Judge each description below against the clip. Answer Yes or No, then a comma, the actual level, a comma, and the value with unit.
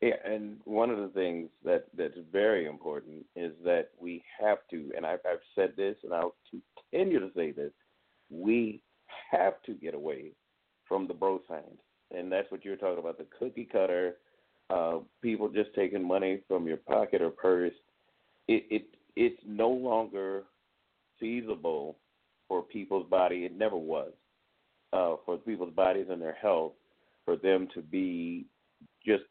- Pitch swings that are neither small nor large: No, wide, 6.0 semitones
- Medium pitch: No, low, 100 Hz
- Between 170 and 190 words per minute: No, average, 160 wpm